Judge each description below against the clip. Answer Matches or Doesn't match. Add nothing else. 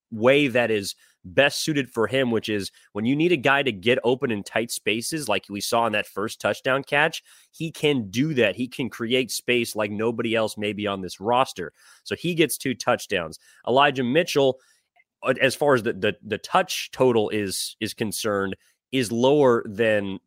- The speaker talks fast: Doesn't match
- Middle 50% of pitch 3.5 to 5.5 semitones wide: Matches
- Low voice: Matches